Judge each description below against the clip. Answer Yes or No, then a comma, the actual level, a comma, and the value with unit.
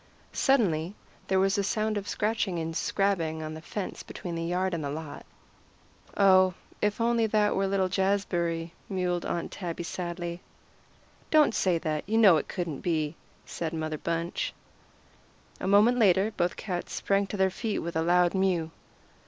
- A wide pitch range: No, average, 3.2 semitones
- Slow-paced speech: No, average, 165 wpm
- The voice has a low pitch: No, medium, 185 Hz